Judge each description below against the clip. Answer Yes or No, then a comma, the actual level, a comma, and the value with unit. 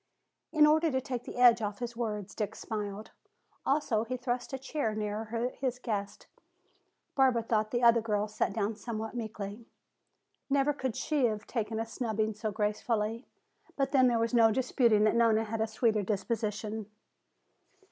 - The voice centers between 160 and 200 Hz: No, high, 225 Hz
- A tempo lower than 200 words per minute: Yes, average, 165 wpm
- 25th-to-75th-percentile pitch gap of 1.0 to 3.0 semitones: Yes, narrow, 2.5 semitones